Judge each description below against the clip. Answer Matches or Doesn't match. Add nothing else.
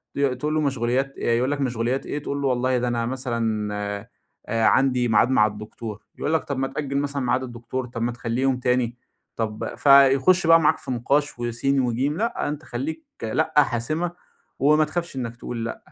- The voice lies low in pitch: Matches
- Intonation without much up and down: Doesn't match